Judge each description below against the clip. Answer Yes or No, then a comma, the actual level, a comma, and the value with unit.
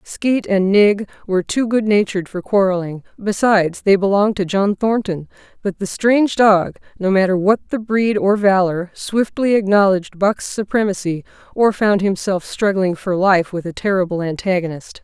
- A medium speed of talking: Yes, average, 150 wpm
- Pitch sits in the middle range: No, high, 195 Hz